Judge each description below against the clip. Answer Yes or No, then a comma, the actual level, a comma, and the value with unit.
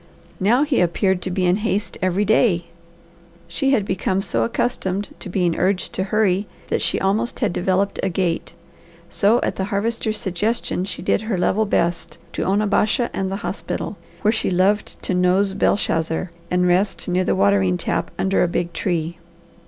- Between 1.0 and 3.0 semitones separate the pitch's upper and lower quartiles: Yes, average, 2.7 semitones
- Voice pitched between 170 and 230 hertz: Yes, high, 190 Hz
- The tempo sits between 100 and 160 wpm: No, average, 175 wpm